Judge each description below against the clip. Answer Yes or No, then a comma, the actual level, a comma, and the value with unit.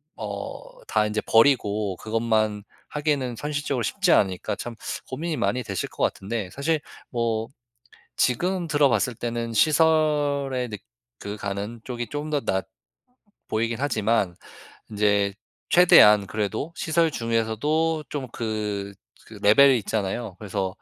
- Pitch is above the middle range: No, low, 115 Hz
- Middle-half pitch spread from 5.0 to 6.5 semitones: Yes, wide, 5.5 semitones